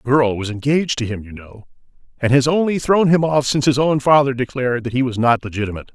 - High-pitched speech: No, low, 130 Hz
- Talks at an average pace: No, fast, 240 wpm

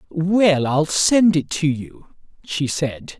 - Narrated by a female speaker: No, male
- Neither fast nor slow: Yes, average, 150 wpm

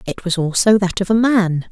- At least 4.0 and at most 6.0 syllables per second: Yes, 5.1 syllables/s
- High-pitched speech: Yes, high, 195 Hz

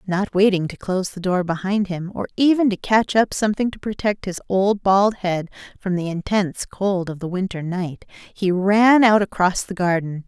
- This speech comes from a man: No, female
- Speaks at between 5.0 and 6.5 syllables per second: No, 4.8 syllables/s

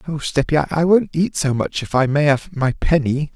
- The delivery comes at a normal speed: No, fast, 230 wpm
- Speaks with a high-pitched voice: No, medium, 150 Hz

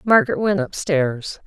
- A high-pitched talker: No, medium, 170 Hz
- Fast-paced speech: No, slow, 125 wpm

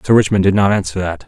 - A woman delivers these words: No, male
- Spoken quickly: Yes, fast, 280 wpm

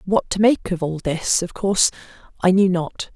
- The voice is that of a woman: Yes, female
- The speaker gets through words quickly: Yes, fast, 210 wpm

